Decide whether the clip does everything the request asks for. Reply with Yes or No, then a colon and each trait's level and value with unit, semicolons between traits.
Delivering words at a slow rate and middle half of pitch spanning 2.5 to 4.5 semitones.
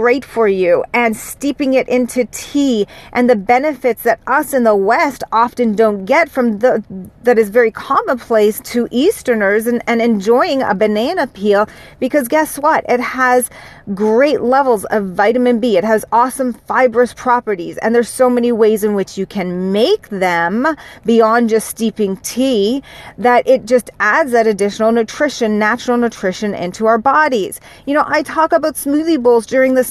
No: average, 170 wpm; average, 3.2 semitones